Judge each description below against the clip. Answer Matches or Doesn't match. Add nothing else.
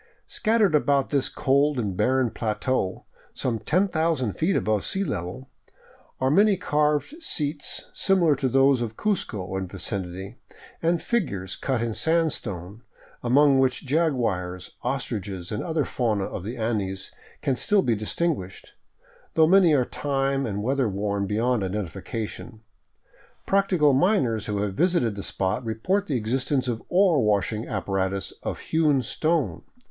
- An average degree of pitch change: Doesn't match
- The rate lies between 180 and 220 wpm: Doesn't match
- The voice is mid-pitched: Doesn't match